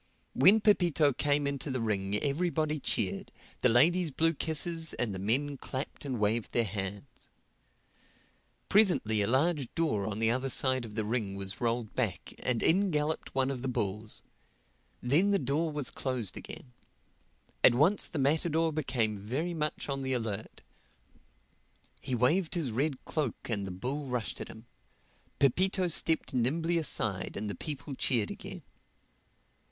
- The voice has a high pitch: No, low, 130 Hz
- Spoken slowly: No, average, 155 wpm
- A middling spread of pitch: No, wide, 5.7 semitones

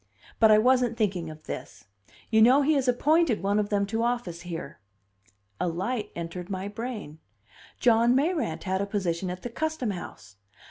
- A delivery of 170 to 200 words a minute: Yes, average, 175 wpm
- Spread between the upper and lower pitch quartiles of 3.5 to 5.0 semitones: No, wide, 5.4 semitones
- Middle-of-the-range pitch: No, high, 210 Hz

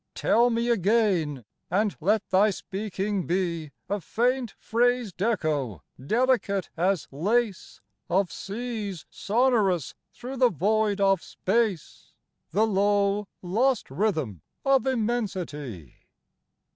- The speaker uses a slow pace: Yes, slow, 105 wpm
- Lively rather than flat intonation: No, average, 4.7 semitones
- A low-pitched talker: No, high, 205 Hz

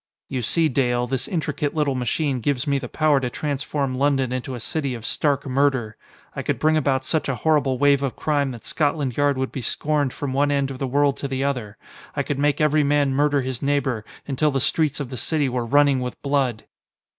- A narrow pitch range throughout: Yes, narrow, 2.1 semitones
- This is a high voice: No, medium, 140 Hz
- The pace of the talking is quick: Yes, fast, 220 wpm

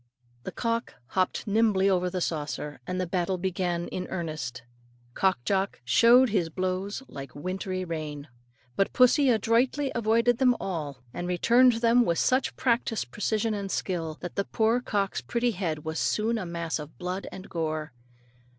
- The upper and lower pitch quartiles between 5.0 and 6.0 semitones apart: Yes, average, 5.3 semitones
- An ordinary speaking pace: Yes, average, 160 wpm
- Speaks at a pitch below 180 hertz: No, high, 190 Hz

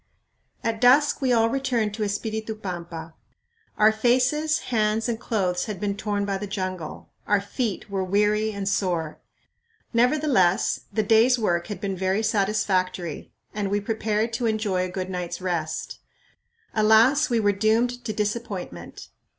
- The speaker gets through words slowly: No, average, 150 wpm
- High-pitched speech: Yes, high, 210 Hz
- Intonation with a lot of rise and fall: No, average, 3.2 semitones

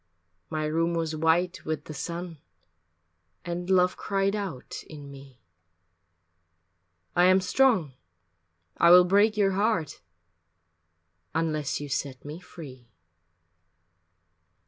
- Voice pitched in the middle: Yes, medium, 165 Hz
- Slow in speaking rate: Yes, slow, 105 wpm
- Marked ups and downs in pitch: No, average, 3.6 semitones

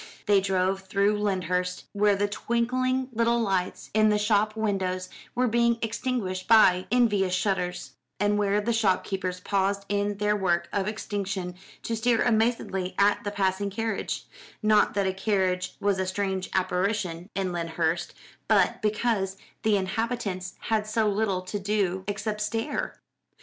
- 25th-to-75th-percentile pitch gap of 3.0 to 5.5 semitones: No, narrow, 2.5 semitones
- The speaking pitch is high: Yes, high, 200 Hz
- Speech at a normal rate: Yes, average, 150 wpm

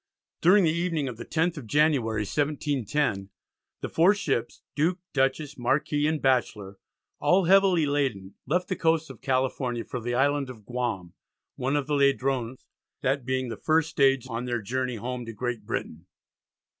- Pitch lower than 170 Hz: Yes, low, 135 Hz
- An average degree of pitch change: Yes, average, 4.1 semitones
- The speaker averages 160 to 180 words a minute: Yes, average, 165 wpm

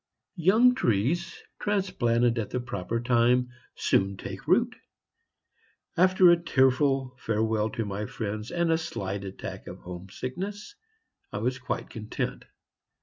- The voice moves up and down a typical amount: No, wide, 7.9 semitones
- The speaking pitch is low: Yes, low, 125 Hz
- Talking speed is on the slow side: Yes, slow, 130 wpm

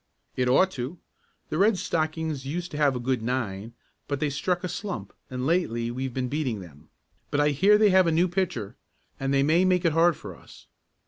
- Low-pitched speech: No, medium, 150 Hz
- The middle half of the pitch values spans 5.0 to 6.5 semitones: Yes, wide, 5.6 semitones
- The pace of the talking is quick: Yes, fast, 210 wpm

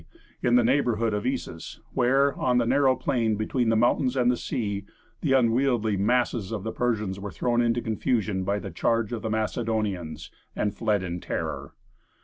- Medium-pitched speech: No, low, 115 Hz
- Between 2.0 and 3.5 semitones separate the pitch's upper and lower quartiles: Yes, average, 2.9 semitones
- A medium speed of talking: Yes, average, 175 wpm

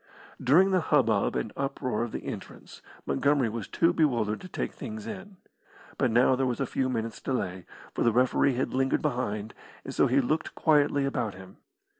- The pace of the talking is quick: No, average, 185 wpm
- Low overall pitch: Yes, low, 130 Hz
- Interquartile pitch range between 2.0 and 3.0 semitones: No, average, 4.4 semitones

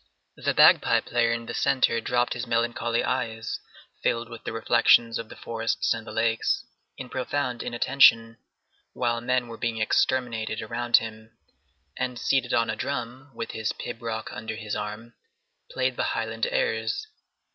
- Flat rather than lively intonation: Yes, narrow, 1.6 semitones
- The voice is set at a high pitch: No, low, 115 Hz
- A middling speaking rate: Yes, average, 155 wpm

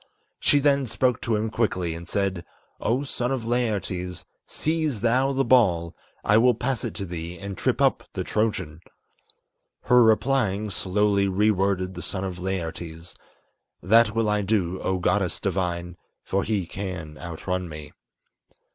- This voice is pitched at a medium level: No, low, 100 Hz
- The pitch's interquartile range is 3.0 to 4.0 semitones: No, average, 4.4 semitones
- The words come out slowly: No, average, 155 wpm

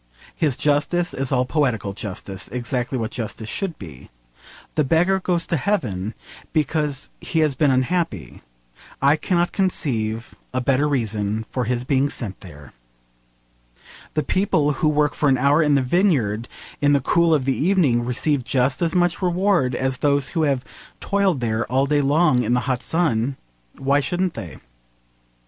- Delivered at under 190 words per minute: Yes, average, 160 wpm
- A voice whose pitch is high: No, medium, 140 Hz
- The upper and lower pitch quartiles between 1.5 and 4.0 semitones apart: No, average, 4.8 semitones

